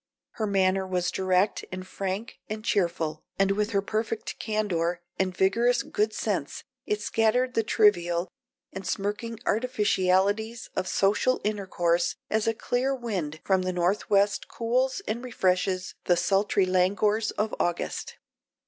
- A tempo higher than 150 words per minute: No, average, 140 wpm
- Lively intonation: No, average, 3.0 semitones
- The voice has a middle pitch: No, high, 200 Hz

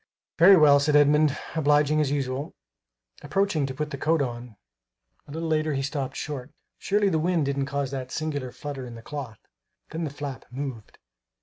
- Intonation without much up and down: Yes, narrow, 2.3 semitones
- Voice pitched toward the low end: No, medium, 145 Hz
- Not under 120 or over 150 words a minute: No, average, 180 wpm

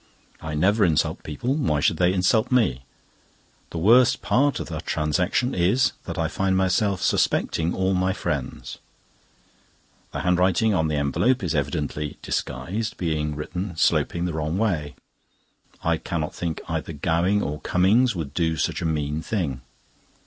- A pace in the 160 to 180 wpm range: No, average, 150 wpm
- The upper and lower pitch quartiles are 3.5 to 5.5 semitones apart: Yes, average, 4.0 semitones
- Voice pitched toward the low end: Yes, very low, 85 Hz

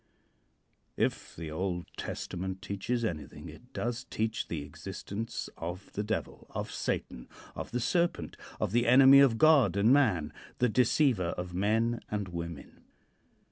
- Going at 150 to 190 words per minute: No, average, 140 wpm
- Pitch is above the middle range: No, low, 105 Hz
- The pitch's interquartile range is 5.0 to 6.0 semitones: Yes, average, 5.3 semitones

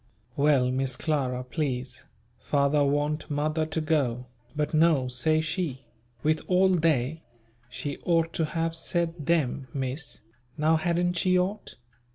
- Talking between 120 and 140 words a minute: Yes, slow, 135 wpm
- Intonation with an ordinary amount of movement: Yes, average, 3.5 semitones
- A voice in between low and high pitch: Yes, medium, 150 Hz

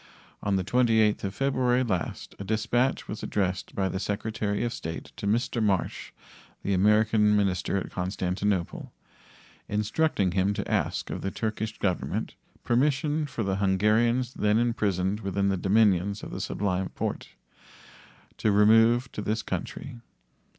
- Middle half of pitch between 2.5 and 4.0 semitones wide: Yes, average, 2.9 semitones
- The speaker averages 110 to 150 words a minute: Yes, average, 145 wpm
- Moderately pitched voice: No, low, 105 Hz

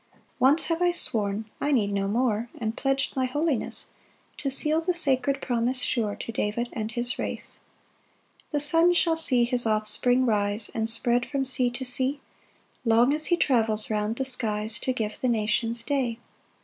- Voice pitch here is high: Yes, high, 245 Hz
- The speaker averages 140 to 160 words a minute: No, average, 180 wpm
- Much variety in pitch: No, average, 3.7 semitones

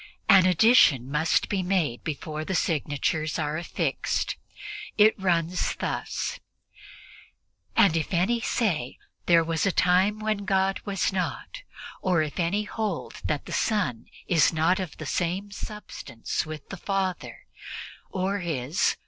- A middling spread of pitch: Yes, average, 3.9 semitones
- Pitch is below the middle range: No, medium, 180 Hz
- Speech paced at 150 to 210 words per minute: No, slow, 135 wpm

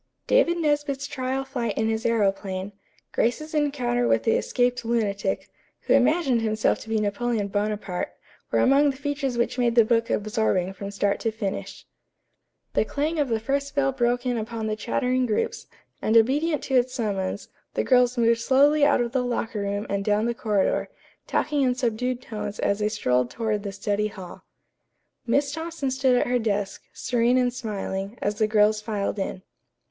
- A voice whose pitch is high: Yes, high, 235 Hz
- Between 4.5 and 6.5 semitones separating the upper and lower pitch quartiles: No, average, 3.9 semitones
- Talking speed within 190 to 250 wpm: No, average, 175 wpm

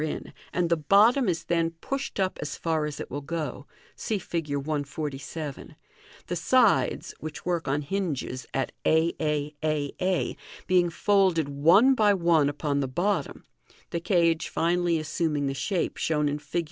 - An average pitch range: Yes, average, 3.3 semitones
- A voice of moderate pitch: Yes, medium, 160 Hz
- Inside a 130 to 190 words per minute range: Yes, average, 160 wpm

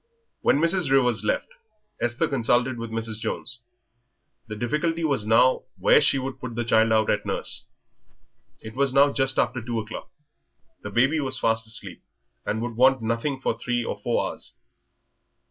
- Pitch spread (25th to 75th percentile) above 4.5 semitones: No, average, 3.0 semitones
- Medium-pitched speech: No, low, 120 Hz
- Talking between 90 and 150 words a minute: No, average, 165 wpm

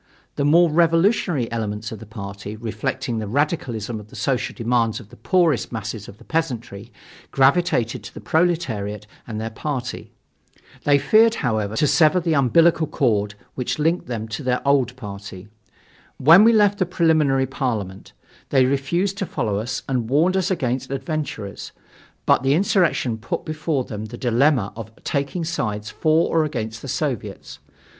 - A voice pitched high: No, low, 130 Hz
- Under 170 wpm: Yes, average, 160 wpm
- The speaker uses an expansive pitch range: Yes, wide, 6.3 semitones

